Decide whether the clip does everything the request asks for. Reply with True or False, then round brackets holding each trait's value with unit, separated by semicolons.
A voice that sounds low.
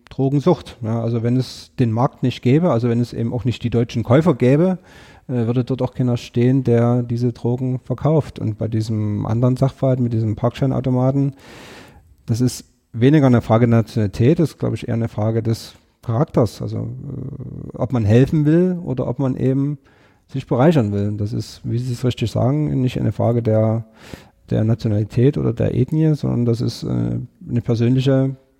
True (120 Hz)